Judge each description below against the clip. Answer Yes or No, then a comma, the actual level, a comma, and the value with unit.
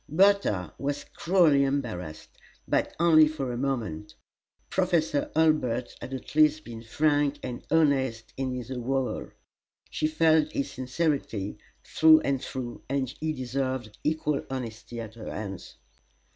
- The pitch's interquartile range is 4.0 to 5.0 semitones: Yes, average, 4.4 semitones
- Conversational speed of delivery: No, slow, 130 wpm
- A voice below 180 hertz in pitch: Yes, low, 135 Hz